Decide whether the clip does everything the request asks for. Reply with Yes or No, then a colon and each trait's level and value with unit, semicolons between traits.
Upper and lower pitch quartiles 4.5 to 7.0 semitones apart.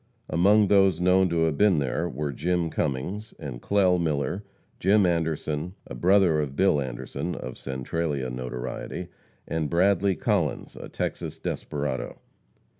Yes: average, 5.1 semitones